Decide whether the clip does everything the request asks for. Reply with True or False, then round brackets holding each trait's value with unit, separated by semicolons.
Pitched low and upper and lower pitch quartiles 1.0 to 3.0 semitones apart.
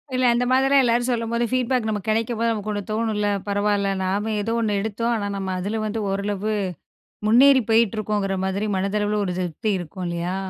False (215 Hz; 2.5 semitones)